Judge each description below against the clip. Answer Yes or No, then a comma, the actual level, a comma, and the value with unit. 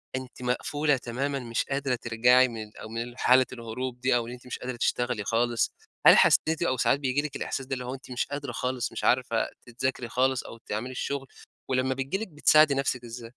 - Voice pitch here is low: Yes, low, 125 Hz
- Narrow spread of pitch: Yes, narrow, 2.0 semitones